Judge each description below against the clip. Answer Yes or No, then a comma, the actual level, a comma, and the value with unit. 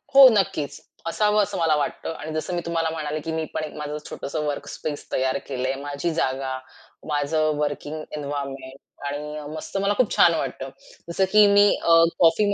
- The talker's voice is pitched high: No, medium, 155 Hz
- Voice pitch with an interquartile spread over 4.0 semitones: No, average, 2.9 semitones